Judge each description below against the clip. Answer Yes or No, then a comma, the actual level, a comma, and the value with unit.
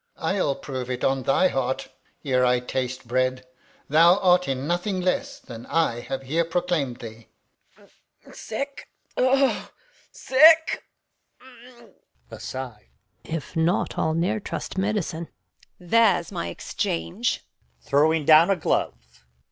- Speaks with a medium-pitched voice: Yes, medium, 160 Hz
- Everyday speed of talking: No, slow, 125 wpm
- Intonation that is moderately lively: No, wide, 6.6 semitones